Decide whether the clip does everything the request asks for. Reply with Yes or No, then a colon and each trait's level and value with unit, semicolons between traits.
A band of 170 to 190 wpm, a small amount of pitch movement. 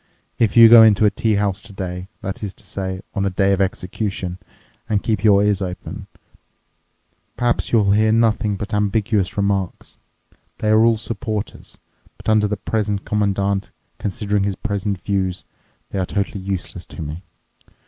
No: average, 155 wpm; narrow, 1.9 semitones